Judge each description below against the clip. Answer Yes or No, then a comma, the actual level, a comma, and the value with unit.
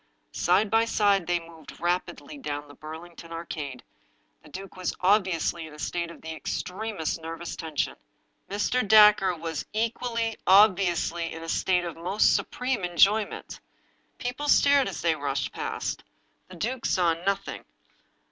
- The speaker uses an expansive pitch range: No, average, 4.2 semitones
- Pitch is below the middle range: No, medium, 180 Hz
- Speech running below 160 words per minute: Yes, average, 150 wpm